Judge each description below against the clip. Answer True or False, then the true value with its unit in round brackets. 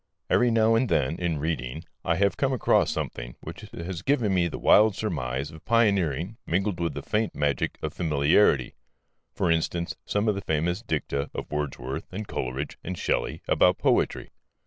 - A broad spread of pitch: True (6.1 semitones)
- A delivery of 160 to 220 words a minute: True (170 wpm)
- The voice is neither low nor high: False (85 Hz)